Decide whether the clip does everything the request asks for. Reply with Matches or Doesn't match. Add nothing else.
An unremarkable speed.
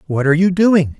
Doesn't match